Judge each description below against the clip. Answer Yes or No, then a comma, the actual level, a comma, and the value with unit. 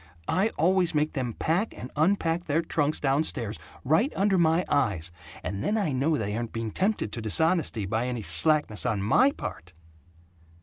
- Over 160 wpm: Yes, average, 175 wpm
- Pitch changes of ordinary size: No, wide, 7.0 semitones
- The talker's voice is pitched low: No, medium, 145 Hz